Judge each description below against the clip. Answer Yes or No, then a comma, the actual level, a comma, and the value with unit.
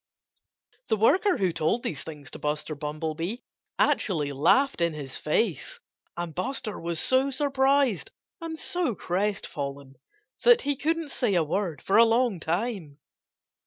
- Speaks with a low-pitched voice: No, high, 190 Hz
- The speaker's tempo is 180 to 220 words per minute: No, average, 140 wpm